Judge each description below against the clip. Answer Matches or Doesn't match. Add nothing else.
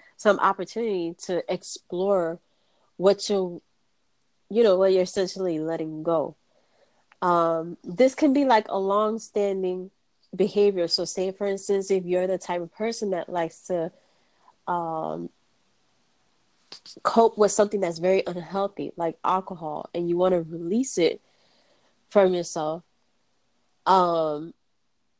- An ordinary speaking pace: Doesn't match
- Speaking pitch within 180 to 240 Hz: Matches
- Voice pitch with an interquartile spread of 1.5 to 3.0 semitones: Matches